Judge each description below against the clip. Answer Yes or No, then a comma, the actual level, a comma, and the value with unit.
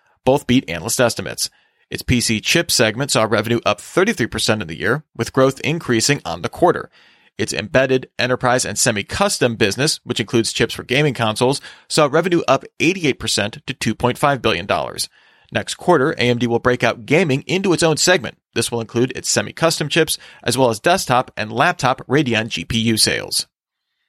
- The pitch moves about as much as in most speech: Yes, average, 4.0 semitones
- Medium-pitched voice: No, low, 125 Hz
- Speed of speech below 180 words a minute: Yes, average, 165 wpm